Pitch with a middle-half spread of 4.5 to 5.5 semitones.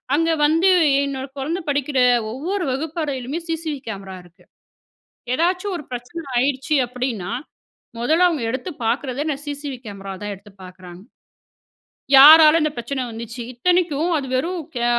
Yes: average, 5.0 semitones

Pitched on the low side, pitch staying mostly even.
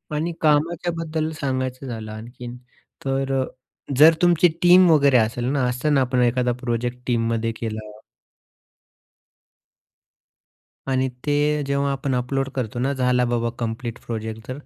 No: low, 130 Hz; average, 3.4 semitones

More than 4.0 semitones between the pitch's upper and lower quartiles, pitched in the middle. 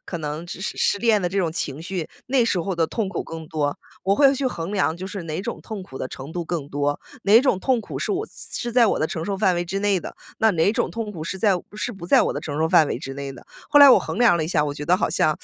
Yes: average, 5.1 semitones; medium, 180 Hz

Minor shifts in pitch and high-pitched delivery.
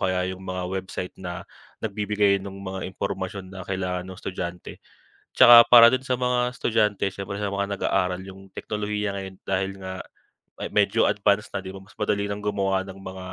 No: narrow, 1.7 semitones; very low, 95 Hz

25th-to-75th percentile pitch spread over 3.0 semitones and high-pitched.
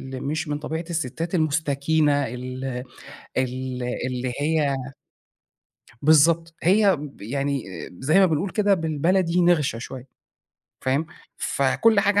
No: average, 3.8 semitones; medium, 150 Hz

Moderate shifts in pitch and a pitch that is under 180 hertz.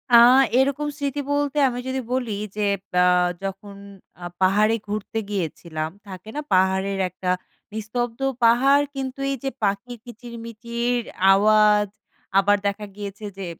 No: average, 3.8 semitones; high, 215 Hz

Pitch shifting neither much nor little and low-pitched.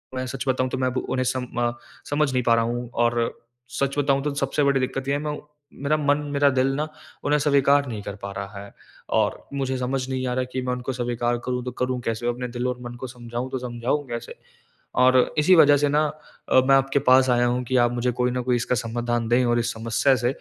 No: narrow, 2.2 semitones; low, 125 Hz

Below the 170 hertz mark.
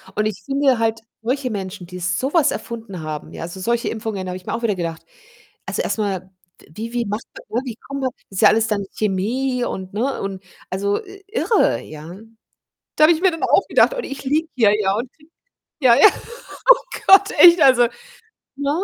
No: high, 225 Hz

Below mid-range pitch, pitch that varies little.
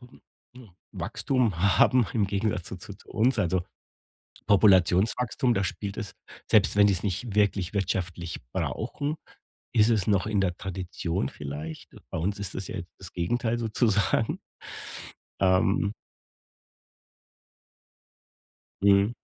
No: low, 100 Hz; average, 3.1 semitones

